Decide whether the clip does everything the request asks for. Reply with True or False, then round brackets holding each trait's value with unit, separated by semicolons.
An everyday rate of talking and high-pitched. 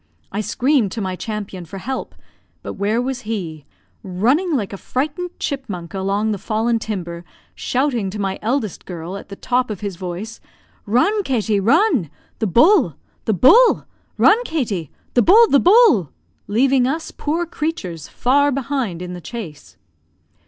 True (155 wpm; 225 Hz)